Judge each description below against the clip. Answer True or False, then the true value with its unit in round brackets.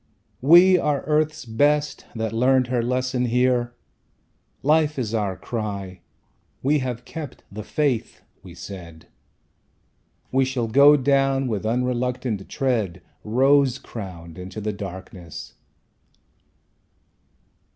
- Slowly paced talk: True (110 wpm)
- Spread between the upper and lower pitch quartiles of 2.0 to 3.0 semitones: False (4.3 semitones)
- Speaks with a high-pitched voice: False (125 Hz)